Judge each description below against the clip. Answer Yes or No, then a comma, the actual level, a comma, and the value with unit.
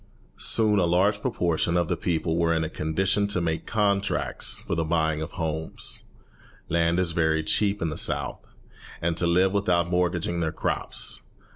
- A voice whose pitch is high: No, very low, 85 Hz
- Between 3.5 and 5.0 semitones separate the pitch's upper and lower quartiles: No, average, 2.8 semitones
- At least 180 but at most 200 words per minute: No, average, 170 wpm